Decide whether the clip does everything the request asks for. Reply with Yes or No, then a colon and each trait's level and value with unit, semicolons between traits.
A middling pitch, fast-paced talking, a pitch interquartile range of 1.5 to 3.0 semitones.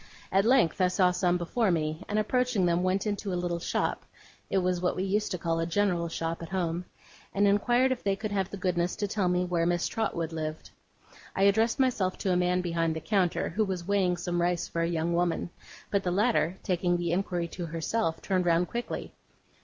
Yes: medium, 180 Hz; fast, 215 wpm; average, 2.7 semitones